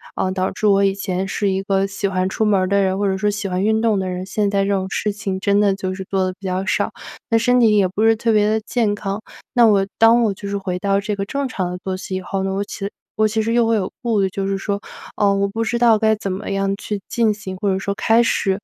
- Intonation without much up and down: Yes, narrow, 2.1 semitones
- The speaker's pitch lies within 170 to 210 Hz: Yes, high, 200 Hz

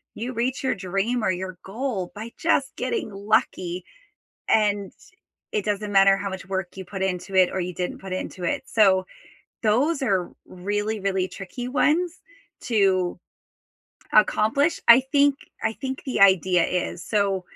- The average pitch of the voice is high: Yes, high, 200 Hz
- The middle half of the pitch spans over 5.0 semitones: No, average, 3.8 semitones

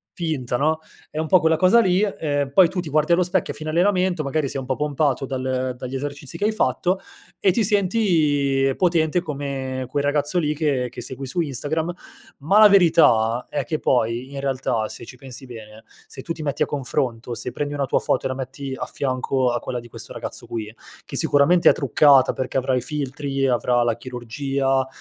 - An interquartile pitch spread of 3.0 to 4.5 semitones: Yes, average, 3.8 semitones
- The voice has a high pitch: No, medium, 140 Hz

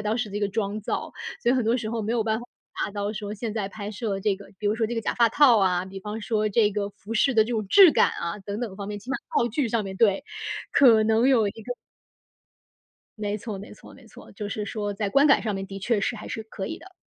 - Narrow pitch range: Yes, narrow, 2.2 semitones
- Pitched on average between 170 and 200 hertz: No, high, 215 Hz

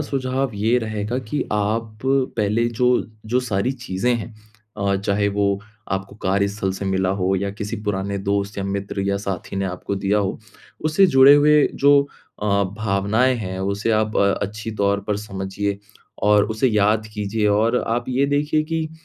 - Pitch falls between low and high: No, low, 105 Hz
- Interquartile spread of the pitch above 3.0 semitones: Yes, average, 3.7 semitones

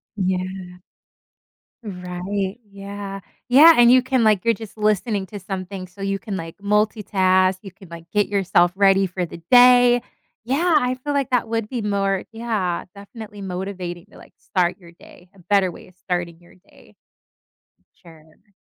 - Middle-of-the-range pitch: No, high, 195 Hz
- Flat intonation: No, average, 3.1 semitones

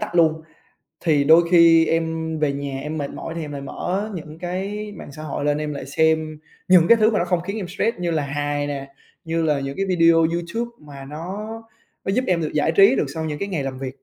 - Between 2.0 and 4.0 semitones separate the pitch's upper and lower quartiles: Yes, average, 3.5 semitones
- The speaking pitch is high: No, medium, 160 Hz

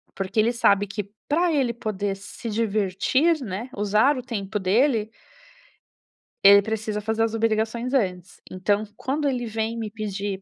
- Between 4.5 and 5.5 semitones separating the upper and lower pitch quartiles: No, average, 2.9 semitones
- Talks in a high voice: Yes, high, 215 Hz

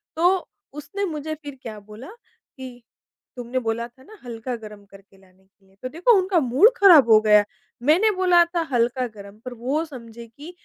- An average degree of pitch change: No, wide, 6.8 semitones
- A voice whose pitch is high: Yes, very high, 250 Hz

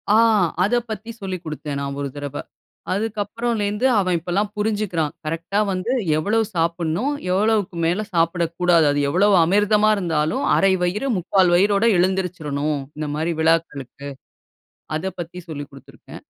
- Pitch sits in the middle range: Yes, medium, 180 Hz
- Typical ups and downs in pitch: Yes, average, 4.4 semitones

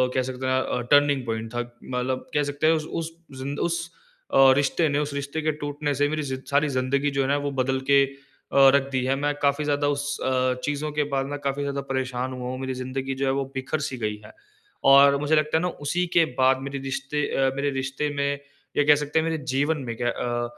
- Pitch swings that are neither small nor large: No, narrow, 1.9 semitones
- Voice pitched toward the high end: No, medium, 140 Hz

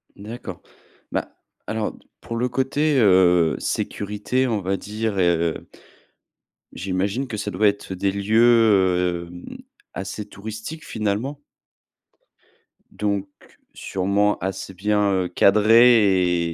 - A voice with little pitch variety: No, average, 3.0 semitones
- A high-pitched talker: No, low, 100 Hz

